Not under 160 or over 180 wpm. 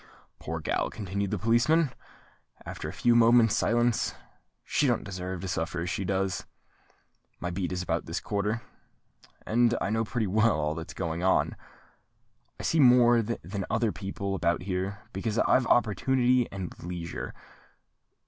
No: average, 150 wpm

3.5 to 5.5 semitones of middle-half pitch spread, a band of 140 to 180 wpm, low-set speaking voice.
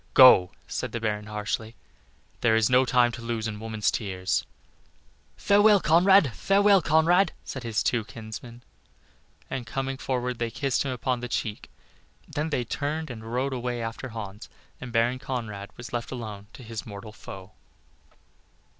No: average, 3.1 semitones; average, 160 wpm; low, 120 Hz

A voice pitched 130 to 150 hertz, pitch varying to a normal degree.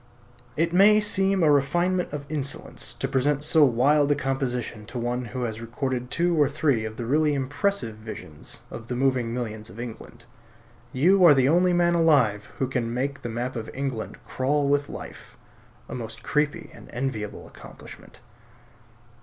Yes: low, 135 Hz; average, 4.0 semitones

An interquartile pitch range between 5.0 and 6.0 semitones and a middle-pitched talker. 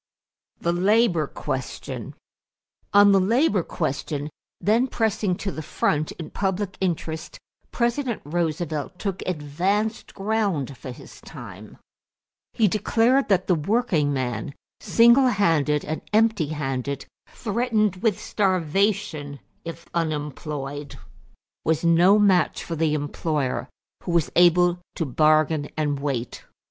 Yes: wide, 5.6 semitones; medium, 170 Hz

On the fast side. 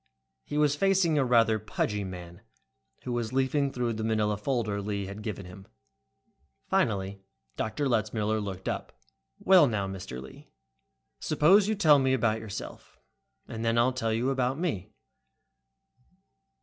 No: average, 150 wpm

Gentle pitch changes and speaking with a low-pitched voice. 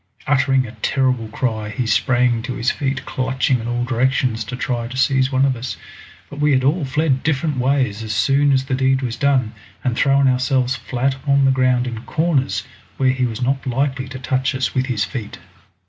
Yes: narrow, 1.8 semitones; low, 130 Hz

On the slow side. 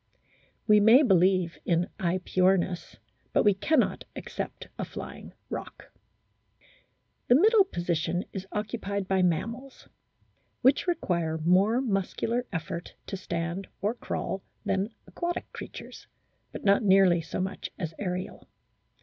Yes: slow, 120 wpm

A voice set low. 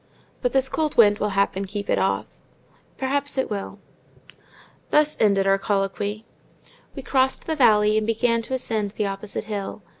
No: high, 215 Hz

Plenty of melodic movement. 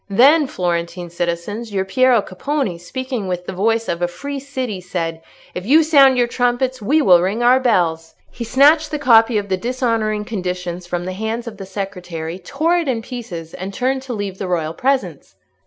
Yes: wide, 6.2 semitones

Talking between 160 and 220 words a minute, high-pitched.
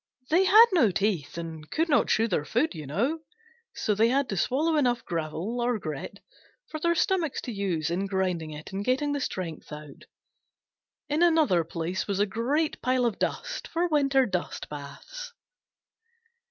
Yes: average, 170 wpm; high, 225 Hz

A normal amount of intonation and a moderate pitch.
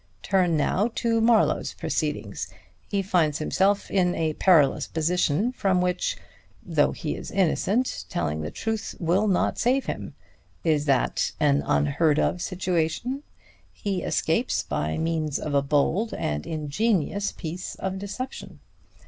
Yes: average, 5.0 semitones; medium, 180 Hz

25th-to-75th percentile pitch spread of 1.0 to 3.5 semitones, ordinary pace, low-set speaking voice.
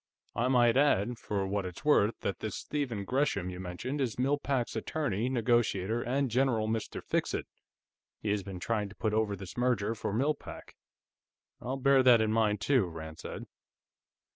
No: average, 4.3 semitones; average, 175 wpm; low, 115 Hz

